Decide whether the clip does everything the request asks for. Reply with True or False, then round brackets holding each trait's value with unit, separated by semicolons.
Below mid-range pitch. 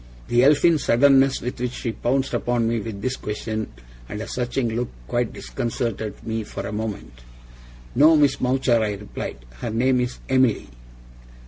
True (120 Hz)